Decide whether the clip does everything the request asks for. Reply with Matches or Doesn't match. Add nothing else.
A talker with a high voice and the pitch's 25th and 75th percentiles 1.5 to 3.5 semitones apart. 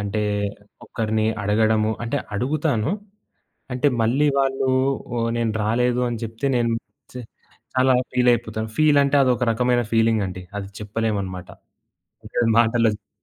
Doesn't match